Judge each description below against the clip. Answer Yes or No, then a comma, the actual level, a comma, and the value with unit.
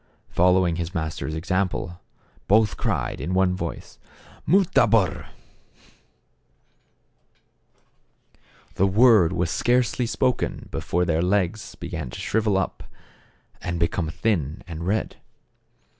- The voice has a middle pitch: No, very low, 90 Hz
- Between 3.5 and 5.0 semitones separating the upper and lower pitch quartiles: Yes, average, 4.1 semitones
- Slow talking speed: Yes, slow, 110 wpm